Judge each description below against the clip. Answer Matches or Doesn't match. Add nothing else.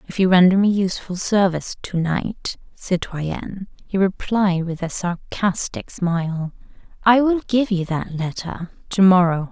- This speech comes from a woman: Matches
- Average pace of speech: Matches